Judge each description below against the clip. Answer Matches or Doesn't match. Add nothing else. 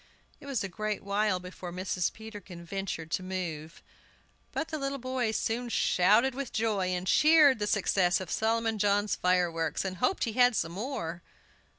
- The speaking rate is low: Doesn't match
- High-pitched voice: Matches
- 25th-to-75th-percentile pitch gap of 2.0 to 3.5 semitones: Doesn't match